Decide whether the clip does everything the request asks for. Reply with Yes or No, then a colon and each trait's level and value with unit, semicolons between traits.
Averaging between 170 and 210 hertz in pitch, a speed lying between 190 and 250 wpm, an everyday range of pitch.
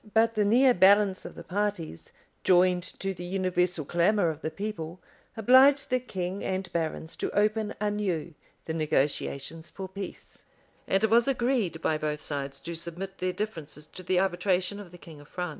No: medium, 185 Hz; average, 175 wpm; average, 4.0 semitones